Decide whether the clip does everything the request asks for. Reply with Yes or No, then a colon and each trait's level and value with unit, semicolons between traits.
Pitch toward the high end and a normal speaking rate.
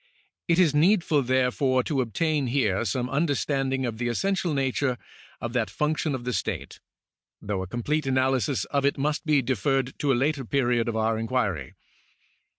No: low, 130 Hz; average, 170 wpm